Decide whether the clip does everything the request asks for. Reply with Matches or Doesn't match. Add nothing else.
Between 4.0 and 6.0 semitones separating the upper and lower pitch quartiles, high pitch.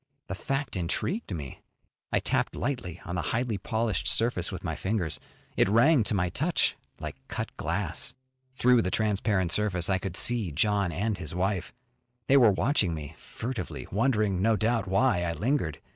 Doesn't match